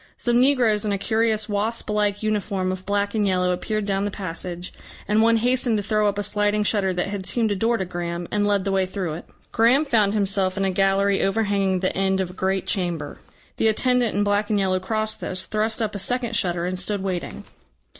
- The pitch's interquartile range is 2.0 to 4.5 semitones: Yes, narrow, 2.4 semitones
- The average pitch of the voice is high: Yes, high, 205 Hz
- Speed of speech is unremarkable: No, fast, 225 wpm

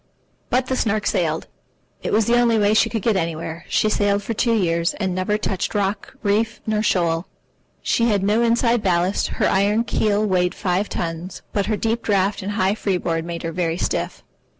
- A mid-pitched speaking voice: No, high, 205 Hz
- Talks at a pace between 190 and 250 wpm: Yes, average, 195 wpm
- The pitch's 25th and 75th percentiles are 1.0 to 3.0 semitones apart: No, average, 3.4 semitones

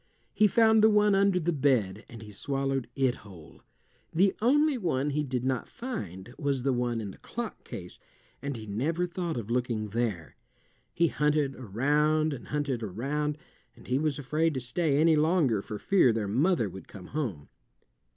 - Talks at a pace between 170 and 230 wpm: Yes, average, 180 wpm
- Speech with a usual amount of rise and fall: No, wide, 6.1 semitones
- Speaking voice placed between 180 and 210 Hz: No, low, 135 Hz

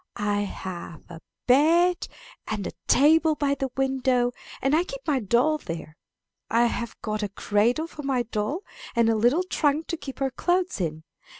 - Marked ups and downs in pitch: Yes, wide, 6.3 semitones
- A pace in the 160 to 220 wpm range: Yes, average, 175 wpm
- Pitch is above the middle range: Yes, very high, 260 Hz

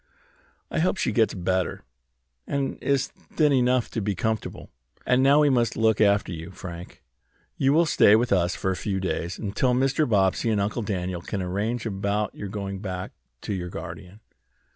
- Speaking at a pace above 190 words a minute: No, average, 175 wpm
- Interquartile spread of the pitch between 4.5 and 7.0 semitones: Yes, average, 4.8 semitones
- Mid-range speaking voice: No, low, 105 Hz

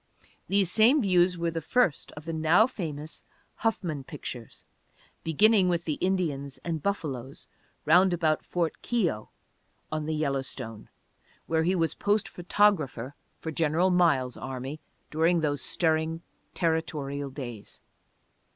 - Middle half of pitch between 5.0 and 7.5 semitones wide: No, average, 3.8 semitones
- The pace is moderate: No, slow, 125 wpm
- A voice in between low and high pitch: Yes, medium, 160 Hz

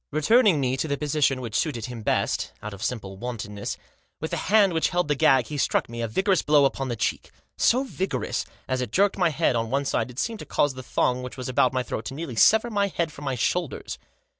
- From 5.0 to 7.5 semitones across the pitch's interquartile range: Yes, wide, 5.4 semitones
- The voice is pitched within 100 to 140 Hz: Yes, low, 135 Hz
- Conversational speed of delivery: No, fast, 250 wpm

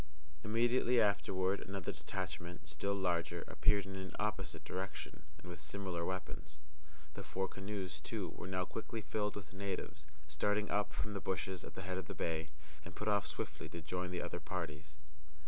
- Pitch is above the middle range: No, very low, 95 Hz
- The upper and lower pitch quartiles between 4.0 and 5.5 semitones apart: No, average, 2.8 semitones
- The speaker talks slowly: No, average, 175 wpm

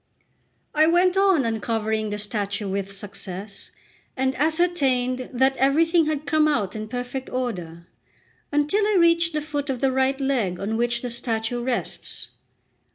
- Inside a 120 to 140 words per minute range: No, average, 150 wpm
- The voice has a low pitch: No, very high, 255 Hz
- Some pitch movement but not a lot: No, wide, 5.8 semitones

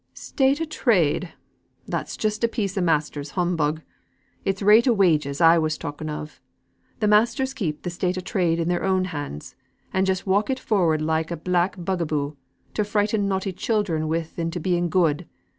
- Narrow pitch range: No, average, 4.3 semitones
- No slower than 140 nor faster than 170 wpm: No, average, 185 wpm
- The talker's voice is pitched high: No, medium, 180 Hz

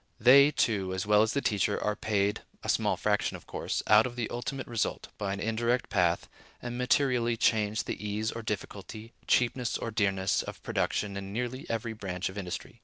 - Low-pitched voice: Yes, low, 110 Hz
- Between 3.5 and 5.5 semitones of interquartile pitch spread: No, average, 3.0 semitones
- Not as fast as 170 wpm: No, average, 190 wpm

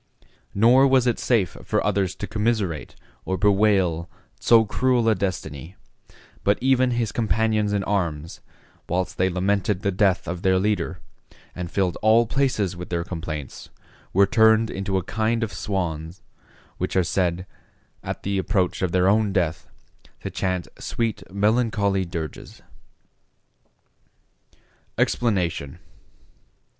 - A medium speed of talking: No, slow, 130 wpm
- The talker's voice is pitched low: Yes, low, 100 Hz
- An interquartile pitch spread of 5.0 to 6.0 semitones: No, average, 3.5 semitones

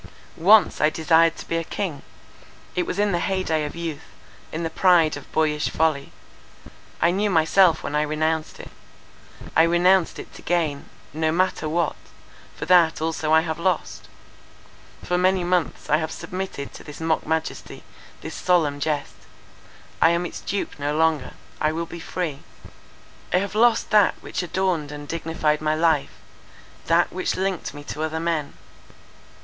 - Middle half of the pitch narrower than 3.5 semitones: Yes, narrow, 2.5 semitones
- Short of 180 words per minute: Yes, average, 165 wpm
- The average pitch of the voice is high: No, medium, 160 Hz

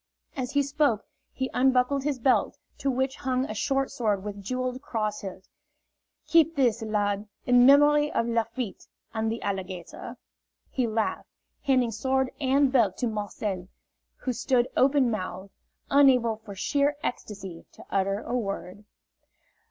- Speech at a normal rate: Yes, average, 145 wpm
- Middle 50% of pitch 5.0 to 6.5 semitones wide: No, average, 4.3 semitones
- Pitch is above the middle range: Yes, high, 240 Hz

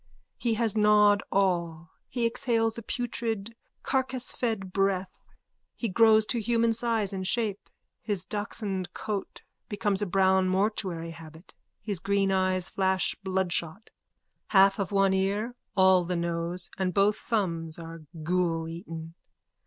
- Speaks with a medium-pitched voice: No, high, 195 Hz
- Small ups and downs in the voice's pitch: No, average, 3.2 semitones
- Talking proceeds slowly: Yes, slow, 130 wpm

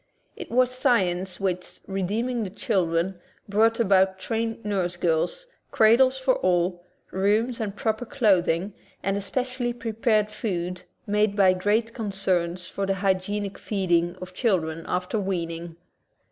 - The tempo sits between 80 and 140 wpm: Yes, slow, 135 wpm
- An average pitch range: Yes, average, 3.7 semitones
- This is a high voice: Yes, high, 195 Hz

